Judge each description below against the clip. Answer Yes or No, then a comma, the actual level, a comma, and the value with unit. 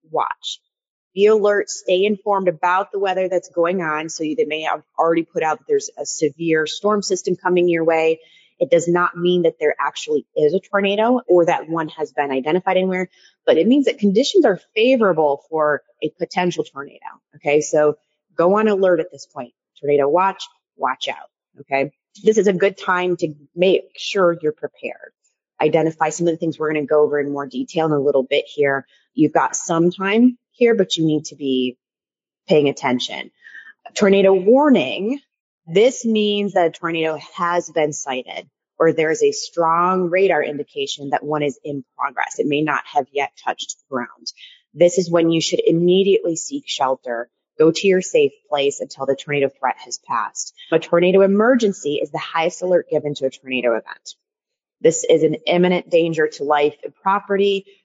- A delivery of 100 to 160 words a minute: No, average, 185 wpm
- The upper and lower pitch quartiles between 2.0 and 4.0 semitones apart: No, average, 4.6 semitones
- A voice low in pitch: No, medium, 170 Hz